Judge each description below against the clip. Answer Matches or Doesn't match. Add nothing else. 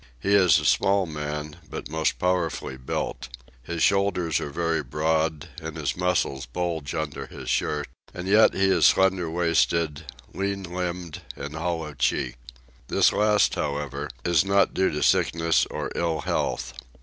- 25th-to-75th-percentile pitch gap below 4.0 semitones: Matches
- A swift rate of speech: Doesn't match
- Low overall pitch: Matches